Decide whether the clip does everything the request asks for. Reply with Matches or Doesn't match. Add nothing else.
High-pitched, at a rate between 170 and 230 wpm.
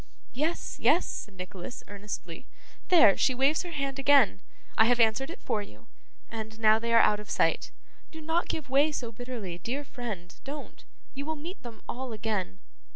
Matches